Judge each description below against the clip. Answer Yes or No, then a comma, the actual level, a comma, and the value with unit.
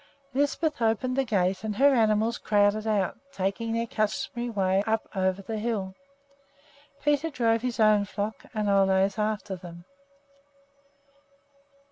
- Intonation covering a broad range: No, average, 2.8 semitones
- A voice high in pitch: Yes, high, 215 Hz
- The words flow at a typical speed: No, slow, 130 wpm